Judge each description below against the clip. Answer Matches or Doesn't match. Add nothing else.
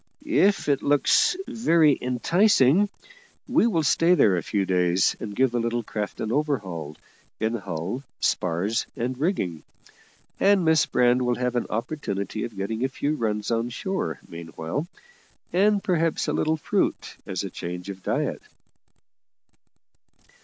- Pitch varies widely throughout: Matches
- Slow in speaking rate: Doesn't match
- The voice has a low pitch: Matches